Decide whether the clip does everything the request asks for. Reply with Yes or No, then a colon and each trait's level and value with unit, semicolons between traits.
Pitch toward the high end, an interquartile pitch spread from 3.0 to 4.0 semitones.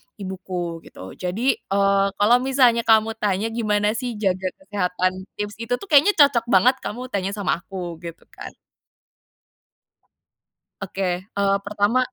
Yes: high, 205 Hz; average, 3.6 semitones